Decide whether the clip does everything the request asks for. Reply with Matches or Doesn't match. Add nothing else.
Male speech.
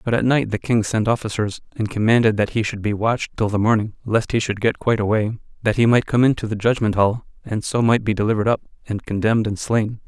Matches